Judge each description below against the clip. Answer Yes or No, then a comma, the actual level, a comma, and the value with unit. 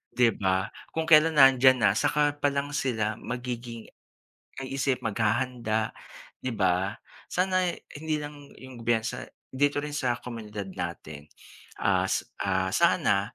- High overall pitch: No, low, 125 Hz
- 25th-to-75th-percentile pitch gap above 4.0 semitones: Yes, average, 4.7 semitones